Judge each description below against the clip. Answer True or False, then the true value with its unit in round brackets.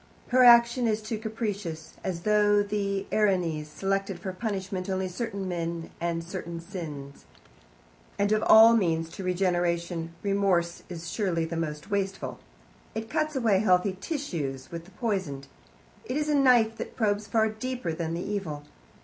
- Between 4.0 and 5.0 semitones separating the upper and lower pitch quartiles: True (4.3 semitones)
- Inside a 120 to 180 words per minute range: True (155 wpm)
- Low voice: False (195 Hz)